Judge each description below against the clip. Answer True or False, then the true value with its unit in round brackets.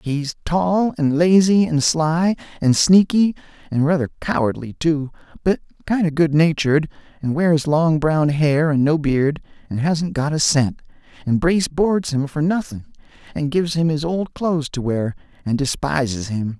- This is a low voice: False (155 Hz)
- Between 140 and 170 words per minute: True (165 wpm)